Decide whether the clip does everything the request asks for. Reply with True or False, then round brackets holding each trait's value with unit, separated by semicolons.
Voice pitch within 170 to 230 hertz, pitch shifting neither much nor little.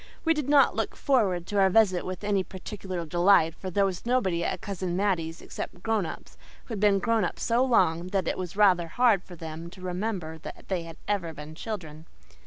True (185 Hz; 3.4 semitones)